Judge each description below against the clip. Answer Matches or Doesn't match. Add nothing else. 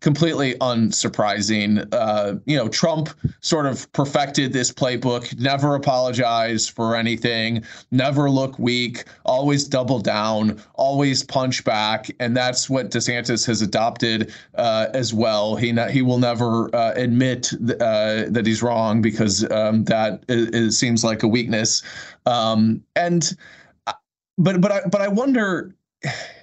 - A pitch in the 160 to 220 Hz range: Doesn't match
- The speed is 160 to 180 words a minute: Doesn't match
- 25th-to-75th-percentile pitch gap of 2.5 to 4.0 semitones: Matches